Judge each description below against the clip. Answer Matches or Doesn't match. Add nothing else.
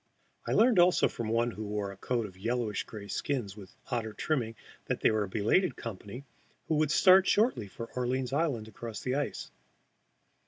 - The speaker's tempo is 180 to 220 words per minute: Matches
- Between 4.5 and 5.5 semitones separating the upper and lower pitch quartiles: Matches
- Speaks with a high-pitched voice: Doesn't match